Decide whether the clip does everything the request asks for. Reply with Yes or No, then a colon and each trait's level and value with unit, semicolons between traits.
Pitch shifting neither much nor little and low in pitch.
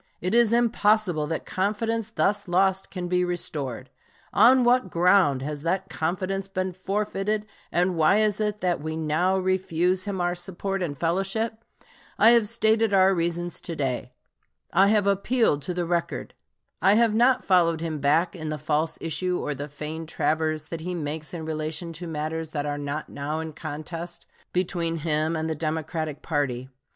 No: average, 3.8 semitones; medium, 175 Hz